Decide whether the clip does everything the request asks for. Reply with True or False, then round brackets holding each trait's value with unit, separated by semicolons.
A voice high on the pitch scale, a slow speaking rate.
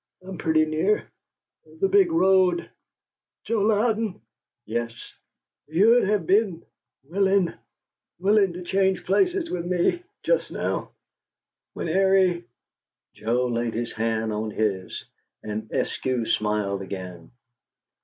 False (170 Hz; 115 wpm)